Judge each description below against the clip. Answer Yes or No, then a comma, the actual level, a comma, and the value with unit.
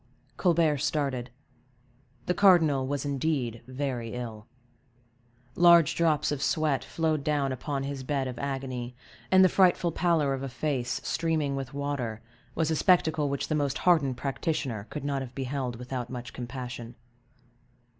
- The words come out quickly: No, average, 145 wpm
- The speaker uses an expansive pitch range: No, average, 3.5 semitones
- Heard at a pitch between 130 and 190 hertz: Yes, medium, 140 Hz